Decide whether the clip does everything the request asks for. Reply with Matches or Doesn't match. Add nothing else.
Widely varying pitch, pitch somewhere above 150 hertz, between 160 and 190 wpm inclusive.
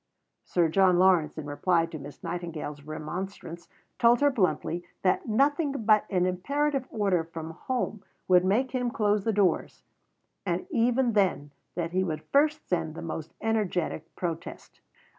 Doesn't match